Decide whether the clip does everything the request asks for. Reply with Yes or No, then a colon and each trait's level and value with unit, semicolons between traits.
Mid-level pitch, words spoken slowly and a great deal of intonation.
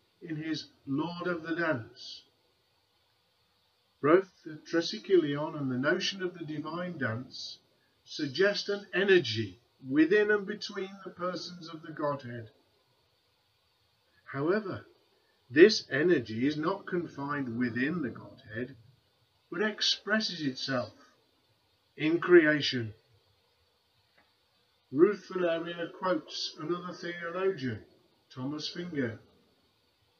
Yes: medium, 155 Hz; slow, 95 wpm; wide, 6.2 semitones